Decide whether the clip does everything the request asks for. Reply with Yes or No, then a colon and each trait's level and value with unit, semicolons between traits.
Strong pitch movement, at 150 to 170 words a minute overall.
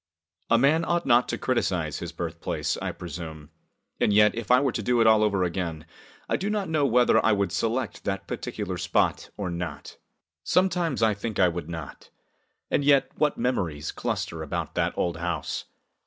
No: wide, 6.7 semitones; average, 185 wpm